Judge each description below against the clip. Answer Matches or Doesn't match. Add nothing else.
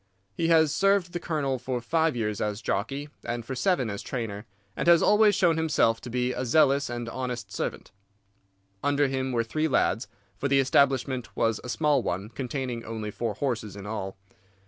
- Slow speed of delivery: Doesn't match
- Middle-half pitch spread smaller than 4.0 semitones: Doesn't match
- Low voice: Matches